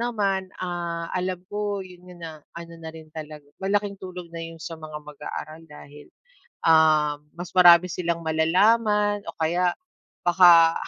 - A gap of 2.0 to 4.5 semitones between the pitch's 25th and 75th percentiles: Yes, average, 2.7 semitones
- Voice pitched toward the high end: No, medium, 170 Hz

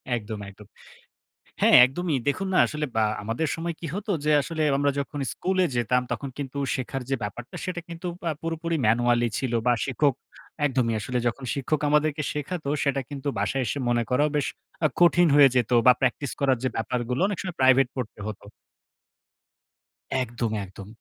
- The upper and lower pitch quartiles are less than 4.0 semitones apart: No, average, 4.4 semitones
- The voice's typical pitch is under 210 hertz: Yes, low, 135 Hz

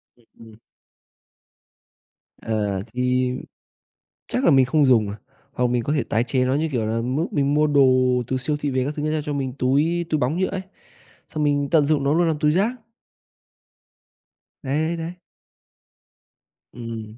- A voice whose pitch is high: No, medium, 140 Hz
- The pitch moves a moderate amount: Yes, average, 3.6 semitones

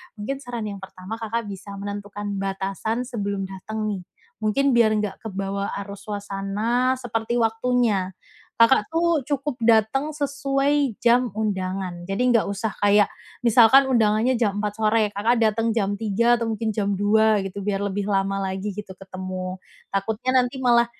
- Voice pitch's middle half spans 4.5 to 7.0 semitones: No, average, 3.1 semitones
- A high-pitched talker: Yes, high, 215 Hz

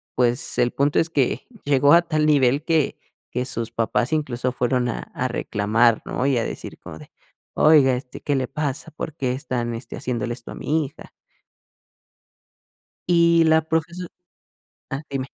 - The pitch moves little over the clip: No, average, 3.9 semitones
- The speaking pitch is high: No, low, 135 Hz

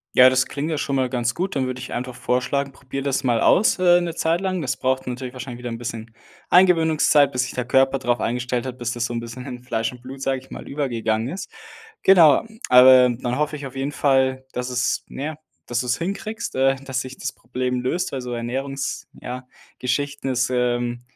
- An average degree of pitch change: No, narrow, 2.1 semitones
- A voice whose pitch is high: No, low, 130 Hz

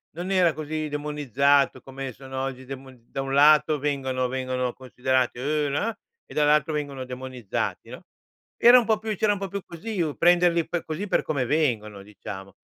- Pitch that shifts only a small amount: No, average, 3.6 semitones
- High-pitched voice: No, medium, 140 Hz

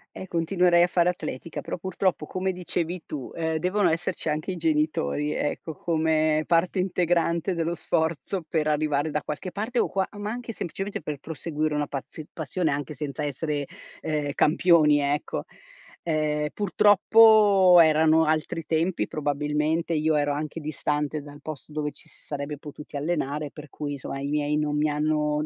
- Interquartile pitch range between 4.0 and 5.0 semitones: No, narrow, 2.6 semitones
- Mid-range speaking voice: Yes, medium, 155 Hz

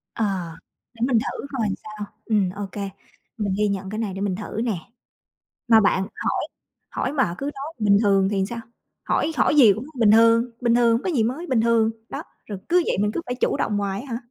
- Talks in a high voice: Yes, high, 220 Hz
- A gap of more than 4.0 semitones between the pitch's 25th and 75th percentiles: No, average, 3.1 semitones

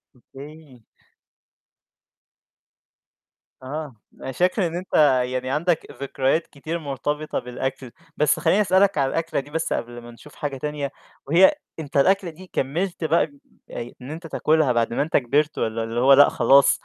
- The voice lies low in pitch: No, medium, 145 Hz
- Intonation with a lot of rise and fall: No, average, 3.7 semitones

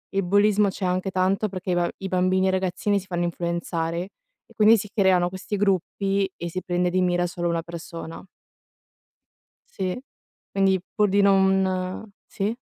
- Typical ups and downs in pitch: No, narrow, 1.8 semitones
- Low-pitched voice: No, medium, 185 Hz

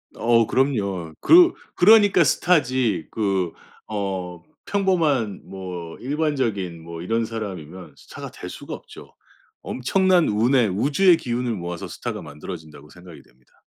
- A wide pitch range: Yes, wide, 7.8 semitones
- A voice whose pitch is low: Yes, low, 110 Hz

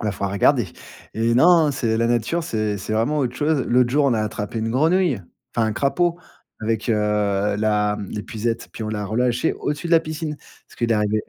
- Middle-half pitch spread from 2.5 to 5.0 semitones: No, wide, 5.4 semitones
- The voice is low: Yes, low, 115 Hz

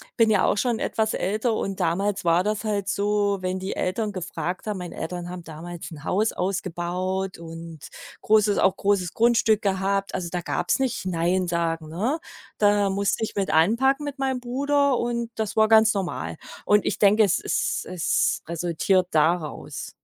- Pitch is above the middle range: Yes, high, 195 Hz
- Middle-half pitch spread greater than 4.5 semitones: No, average, 3.6 semitones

